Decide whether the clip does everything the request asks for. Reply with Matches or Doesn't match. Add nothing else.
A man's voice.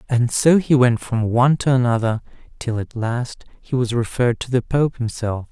Matches